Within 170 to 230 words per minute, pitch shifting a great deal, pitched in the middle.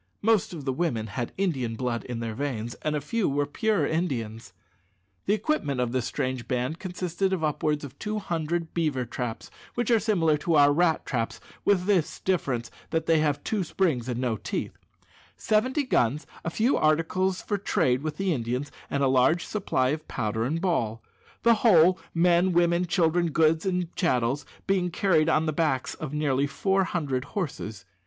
Yes: average, 180 wpm; wide, 5.9 semitones; medium, 155 Hz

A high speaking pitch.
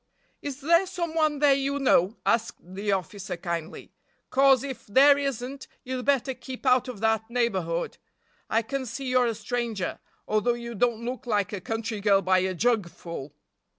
Yes: high, 235 Hz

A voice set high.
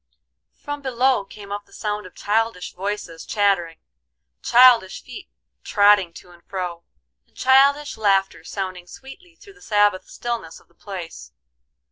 Yes: high, 205 Hz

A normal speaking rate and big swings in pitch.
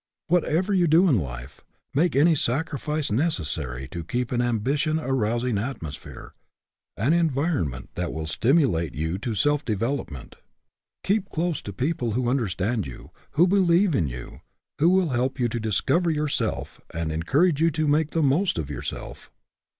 Yes: average, 160 wpm; wide, 9.0 semitones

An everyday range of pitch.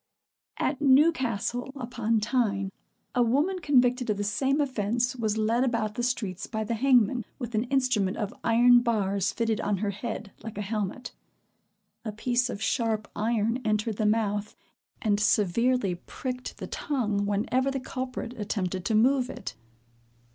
Yes: average, 3.2 semitones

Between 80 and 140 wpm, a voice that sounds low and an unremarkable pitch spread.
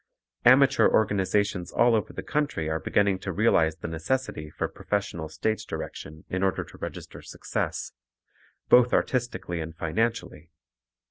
No: slow, 135 wpm; very low, 95 Hz; wide, 6.1 semitones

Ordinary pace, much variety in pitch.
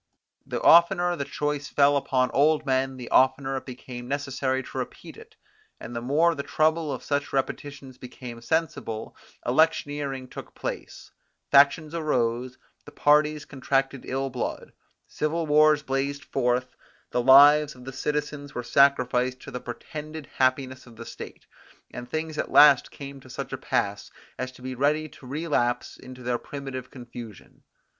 No: average, 155 wpm; average, 2.7 semitones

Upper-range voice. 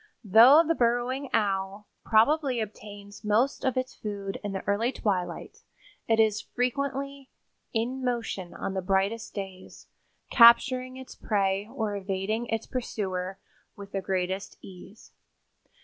Yes: high, 215 Hz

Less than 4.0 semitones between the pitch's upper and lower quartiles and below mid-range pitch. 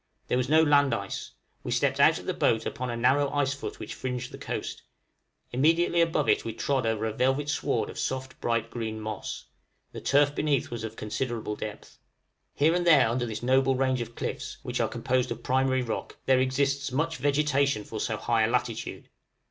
Yes: average, 3.5 semitones; low, 130 Hz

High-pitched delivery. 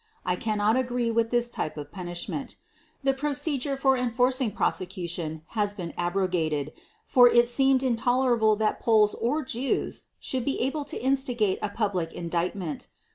Yes: high, 230 Hz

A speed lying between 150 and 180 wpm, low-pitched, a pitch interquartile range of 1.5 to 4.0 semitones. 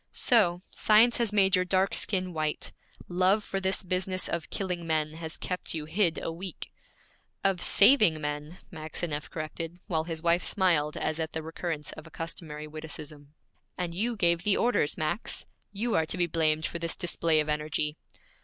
No: average, 175 wpm; medium, 170 Hz; average, 3.2 semitones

